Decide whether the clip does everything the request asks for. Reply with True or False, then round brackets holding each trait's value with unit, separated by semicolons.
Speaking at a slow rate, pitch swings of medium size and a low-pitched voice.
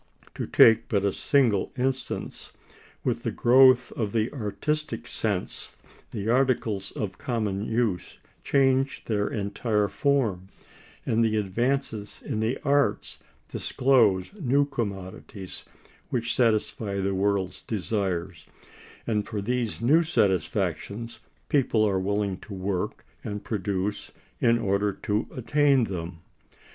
True (120 wpm; 4.1 semitones; 110 Hz)